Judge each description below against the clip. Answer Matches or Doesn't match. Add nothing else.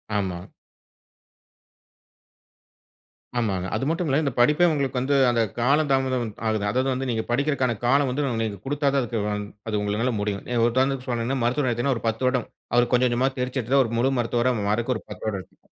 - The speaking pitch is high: Doesn't match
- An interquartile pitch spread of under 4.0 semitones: Matches